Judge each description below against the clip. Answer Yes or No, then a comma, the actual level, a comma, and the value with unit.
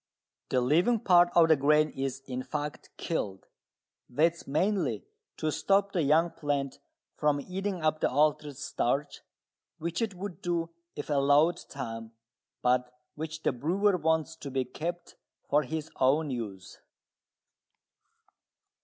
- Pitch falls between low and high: Yes, medium, 150 Hz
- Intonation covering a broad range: No, average, 3.8 semitones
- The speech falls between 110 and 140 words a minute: Yes, slow, 135 wpm